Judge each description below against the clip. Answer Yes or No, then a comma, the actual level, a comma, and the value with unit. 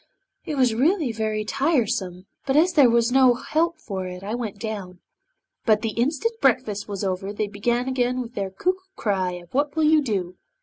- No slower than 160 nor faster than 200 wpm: Yes, average, 185 wpm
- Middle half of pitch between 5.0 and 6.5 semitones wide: Yes, wide, 5.4 semitones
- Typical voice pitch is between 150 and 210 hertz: No, high, 235 Hz